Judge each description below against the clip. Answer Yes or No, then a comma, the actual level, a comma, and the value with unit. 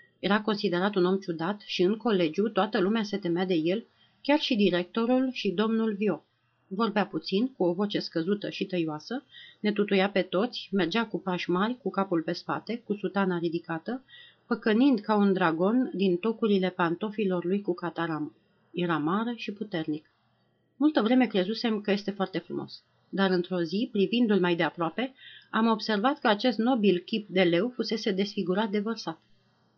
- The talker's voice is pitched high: Yes, high, 195 Hz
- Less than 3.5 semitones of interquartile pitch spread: No, average, 4.2 semitones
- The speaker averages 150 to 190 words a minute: Yes, average, 165 wpm